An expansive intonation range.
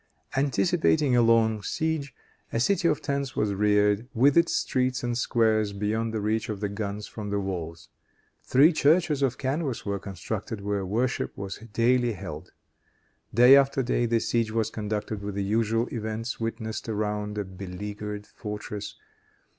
No: average, 3.6 semitones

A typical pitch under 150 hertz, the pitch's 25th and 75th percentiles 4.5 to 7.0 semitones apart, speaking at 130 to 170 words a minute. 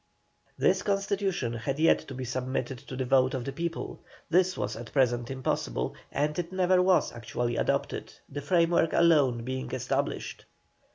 Yes: low, 135 Hz; average, 5.2 semitones; average, 160 wpm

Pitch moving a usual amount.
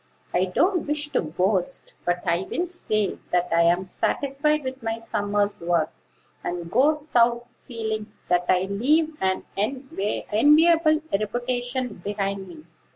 No: wide, 6.6 semitones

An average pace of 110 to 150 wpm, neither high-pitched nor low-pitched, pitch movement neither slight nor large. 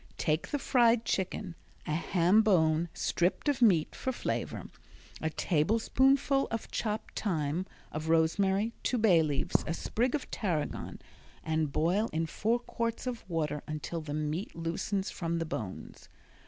No: average, 145 wpm; medium, 175 Hz; wide, 6.0 semitones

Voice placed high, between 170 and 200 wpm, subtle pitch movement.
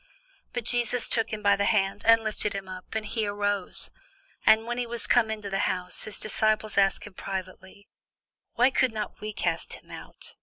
Yes: high, 215 Hz; average, 195 wpm; narrow, 2.2 semitones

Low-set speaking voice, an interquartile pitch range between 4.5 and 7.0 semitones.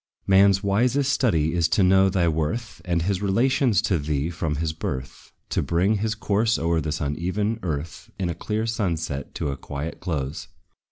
Yes: very low, 90 Hz; average, 4.9 semitones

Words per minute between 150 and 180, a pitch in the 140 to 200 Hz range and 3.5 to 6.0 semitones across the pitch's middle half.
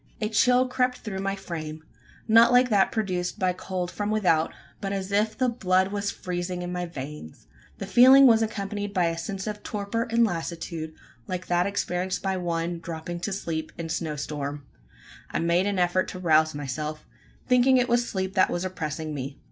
No: average, 190 wpm; medium, 185 Hz; average, 4.0 semitones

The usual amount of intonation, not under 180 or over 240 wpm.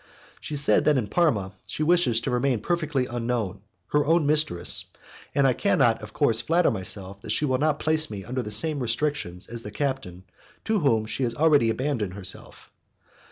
No: wide, 5.7 semitones; average, 185 wpm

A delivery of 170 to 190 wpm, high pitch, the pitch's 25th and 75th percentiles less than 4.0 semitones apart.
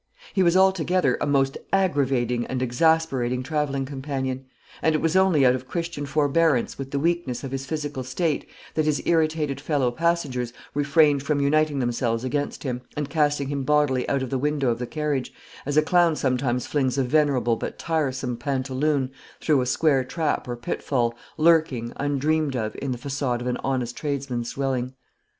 No: average, 175 wpm; medium, 140 Hz; average, 3.2 semitones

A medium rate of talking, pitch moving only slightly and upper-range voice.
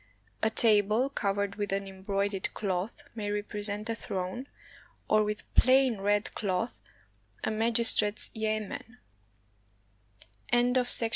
No: slow, 100 wpm; narrow, 2.0 semitones; high, 210 Hz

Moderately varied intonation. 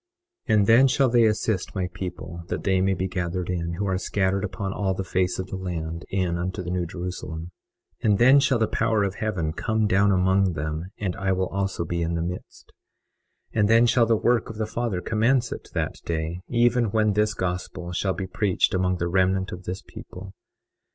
Yes: average, 3.1 semitones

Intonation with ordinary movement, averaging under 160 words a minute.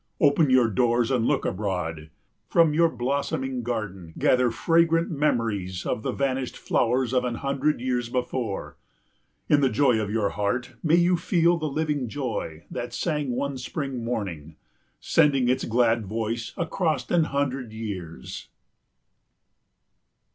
Yes: average, 4.3 semitones; average, 140 wpm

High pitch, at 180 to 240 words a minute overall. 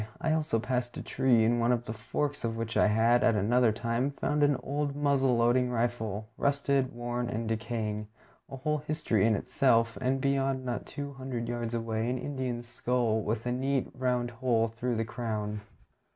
No: low, 120 Hz; average, 185 wpm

